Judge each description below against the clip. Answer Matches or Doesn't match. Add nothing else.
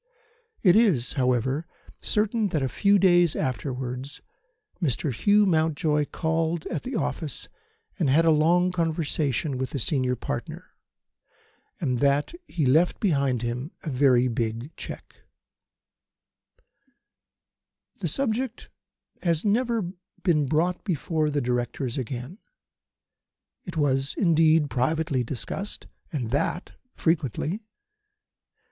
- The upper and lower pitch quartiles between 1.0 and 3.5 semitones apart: Doesn't match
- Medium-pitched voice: Matches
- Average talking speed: Doesn't match